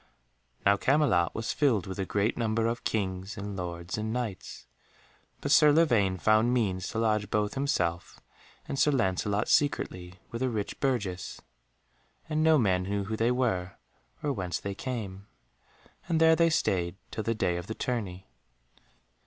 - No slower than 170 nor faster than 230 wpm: No, average, 160 wpm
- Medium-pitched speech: No, low, 105 Hz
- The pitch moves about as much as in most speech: Yes, average, 4.9 semitones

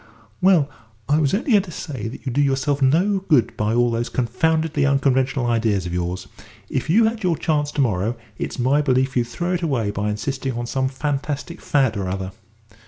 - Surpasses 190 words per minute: Yes, average, 200 wpm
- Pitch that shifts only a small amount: No, average, 4.6 semitones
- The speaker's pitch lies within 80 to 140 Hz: Yes, low, 135 Hz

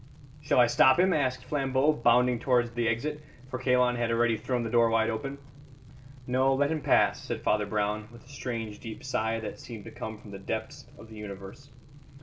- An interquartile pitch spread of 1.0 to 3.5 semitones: Yes, average, 2.9 semitones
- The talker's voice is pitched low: Yes, low, 120 Hz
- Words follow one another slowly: No, average, 200 wpm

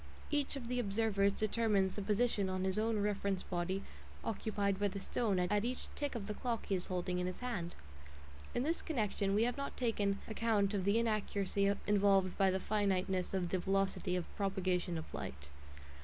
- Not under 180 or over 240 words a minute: Yes, average, 185 wpm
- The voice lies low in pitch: No, high, 200 Hz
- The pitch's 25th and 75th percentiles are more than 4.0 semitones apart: No, average, 2.8 semitones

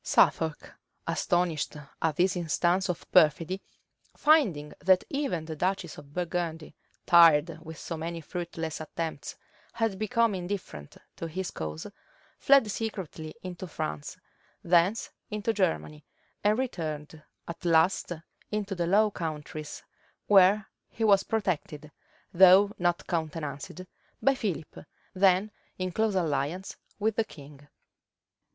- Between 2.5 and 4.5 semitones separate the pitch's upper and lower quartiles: Yes, average, 3.8 semitones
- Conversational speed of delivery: No, slow, 120 wpm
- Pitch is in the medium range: Yes, medium, 175 Hz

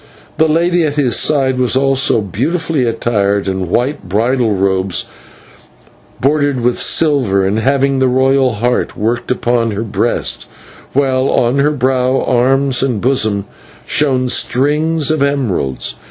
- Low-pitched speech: Yes, low, 130 Hz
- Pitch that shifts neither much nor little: Yes, average, 3.6 semitones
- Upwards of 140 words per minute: No, slow, 135 wpm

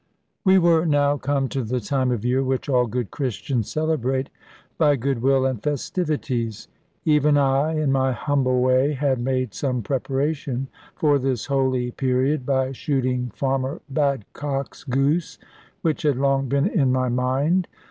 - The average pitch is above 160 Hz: No, low, 135 Hz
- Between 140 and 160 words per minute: Yes, average, 145 wpm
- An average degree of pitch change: No, narrow, 2.1 semitones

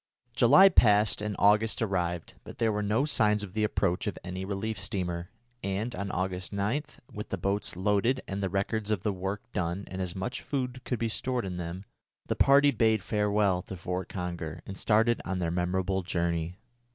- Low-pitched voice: Yes, low, 100 Hz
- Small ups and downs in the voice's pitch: No, average, 3.0 semitones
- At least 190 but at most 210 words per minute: Yes, average, 195 wpm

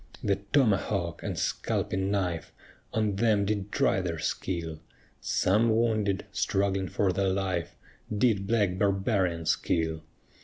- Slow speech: Yes, slow, 120 wpm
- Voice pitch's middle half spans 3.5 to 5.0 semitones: No, narrow, 2.4 semitones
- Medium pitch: No, very low, 95 Hz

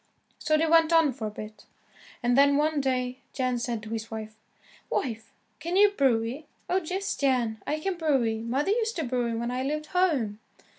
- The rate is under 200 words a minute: No, fast, 205 wpm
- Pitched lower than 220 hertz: No, very high, 265 Hz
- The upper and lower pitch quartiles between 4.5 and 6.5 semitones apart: Yes, wide, 5.5 semitones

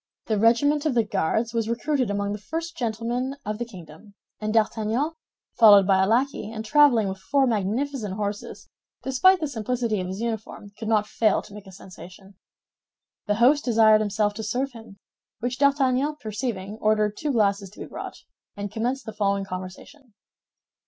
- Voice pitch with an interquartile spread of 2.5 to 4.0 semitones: Yes, average, 3.7 semitones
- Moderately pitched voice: No, high, 220 Hz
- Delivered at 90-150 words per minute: No, average, 170 wpm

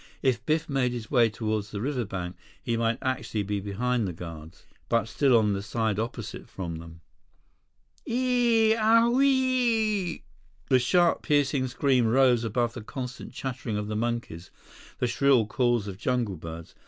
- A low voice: Yes, low, 120 Hz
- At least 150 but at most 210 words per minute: Yes, average, 155 wpm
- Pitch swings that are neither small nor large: Yes, average, 5.0 semitones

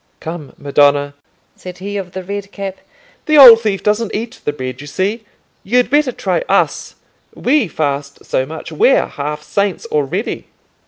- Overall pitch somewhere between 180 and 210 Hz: Yes, high, 190 Hz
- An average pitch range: No, wide, 7.4 semitones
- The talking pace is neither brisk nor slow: Yes, average, 160 wpm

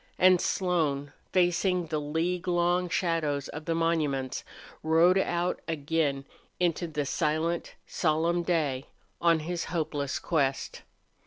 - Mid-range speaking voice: Yes, medium, 165 Hz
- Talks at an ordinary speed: No, slow, 115 wpm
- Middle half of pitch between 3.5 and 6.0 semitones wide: No, average, 2.7 semitones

